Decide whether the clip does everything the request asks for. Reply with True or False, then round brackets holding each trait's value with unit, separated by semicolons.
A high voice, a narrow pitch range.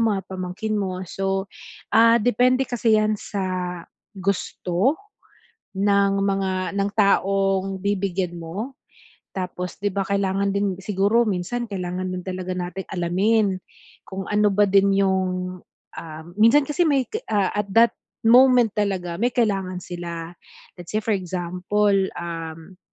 True (195 Hz; 2.3 semitones)